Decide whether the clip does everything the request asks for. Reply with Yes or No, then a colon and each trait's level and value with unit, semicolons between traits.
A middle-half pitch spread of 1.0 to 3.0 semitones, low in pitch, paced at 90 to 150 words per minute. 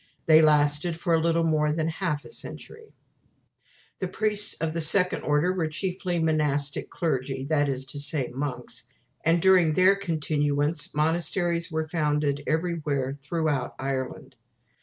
No: average, 2.7 semitones; medium, 155 Hz; average, 140 wpm